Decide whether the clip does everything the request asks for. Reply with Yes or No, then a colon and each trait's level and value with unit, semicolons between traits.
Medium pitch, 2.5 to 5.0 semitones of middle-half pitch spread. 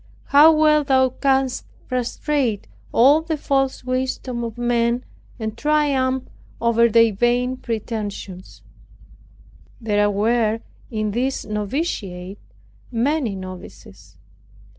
No: high, 240 Hz; average, 3.8 semitones